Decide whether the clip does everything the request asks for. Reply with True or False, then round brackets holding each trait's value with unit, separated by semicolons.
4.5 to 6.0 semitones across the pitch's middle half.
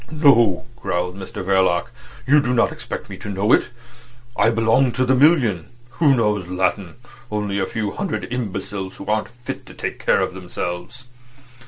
True (4.9 semitones)